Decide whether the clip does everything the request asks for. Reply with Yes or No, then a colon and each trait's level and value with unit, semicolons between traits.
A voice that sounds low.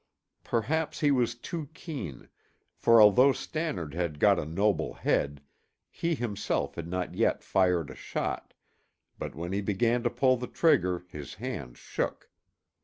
Yes: low, 105 Hz